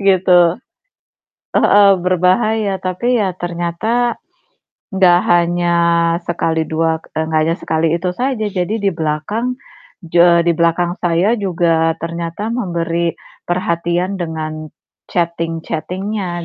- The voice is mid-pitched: Yes, medium, 175 Hz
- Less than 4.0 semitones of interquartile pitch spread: Yes, narrow, 2.5 semitones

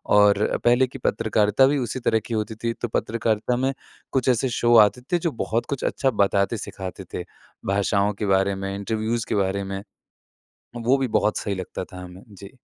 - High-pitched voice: No, low, 110 Hz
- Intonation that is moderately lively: Yes, average, 3.3 semitones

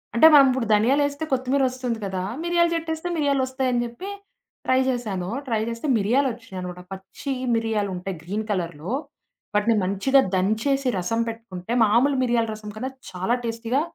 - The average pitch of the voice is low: No, high, 230 Hz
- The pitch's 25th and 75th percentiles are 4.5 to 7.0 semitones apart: Yes, average, 4.8 semitones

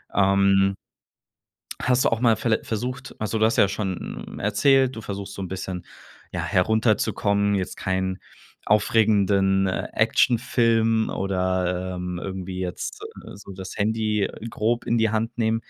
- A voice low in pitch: Yes, low, 100 Hz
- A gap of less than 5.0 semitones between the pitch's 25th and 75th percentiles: Yes, average, 2.8 semitones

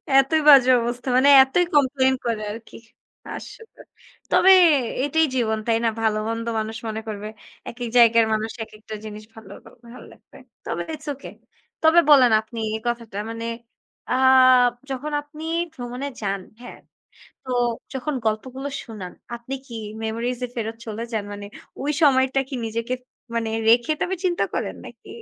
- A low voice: No, high, 240 Hz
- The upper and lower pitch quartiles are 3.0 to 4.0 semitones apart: Yes, average, 3.5 semitones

